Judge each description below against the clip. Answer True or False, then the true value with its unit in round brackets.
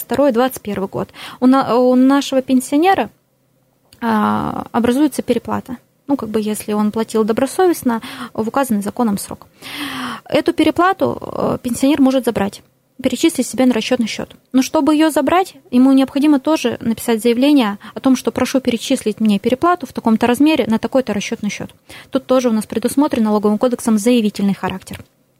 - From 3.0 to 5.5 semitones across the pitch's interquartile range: True (3.5 semitones)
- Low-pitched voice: False (245 Hz)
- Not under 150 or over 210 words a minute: False (140 wpm)